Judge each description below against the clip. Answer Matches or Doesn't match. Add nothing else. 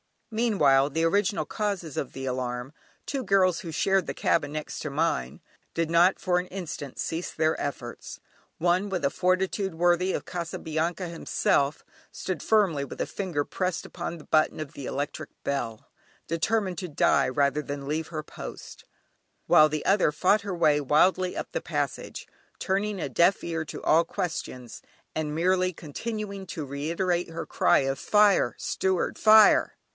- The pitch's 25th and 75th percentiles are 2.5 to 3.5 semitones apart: Doesn't match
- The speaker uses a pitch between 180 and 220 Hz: Doesn't match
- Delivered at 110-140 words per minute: Doesn't match